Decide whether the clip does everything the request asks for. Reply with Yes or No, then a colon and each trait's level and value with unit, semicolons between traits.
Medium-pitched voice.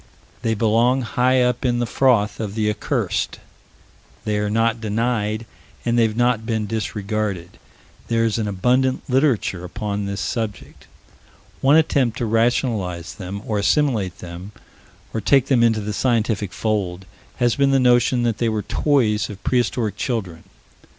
No: low, 110 Hz